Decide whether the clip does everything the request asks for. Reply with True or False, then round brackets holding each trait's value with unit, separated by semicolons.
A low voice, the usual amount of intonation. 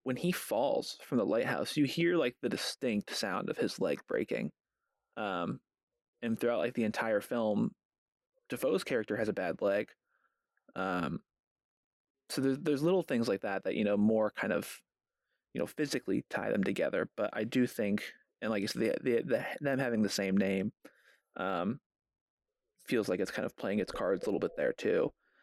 False (130 Hz; 8.4 semitones)